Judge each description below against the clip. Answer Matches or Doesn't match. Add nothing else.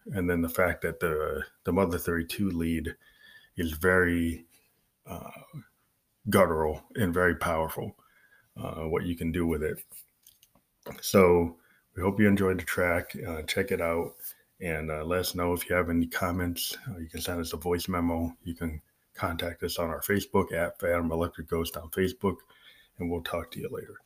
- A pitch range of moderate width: Doesn't match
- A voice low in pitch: Matches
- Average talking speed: Matches